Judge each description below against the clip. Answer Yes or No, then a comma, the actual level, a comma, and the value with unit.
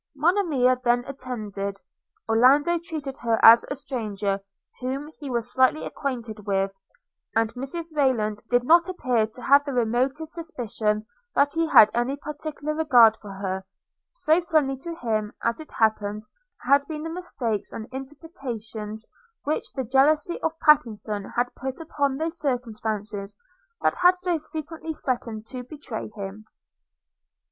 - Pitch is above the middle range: Yes, very high, 255 Hz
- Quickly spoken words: No, average, 140 wpm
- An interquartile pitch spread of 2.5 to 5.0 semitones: No, wide, 5.6 semitones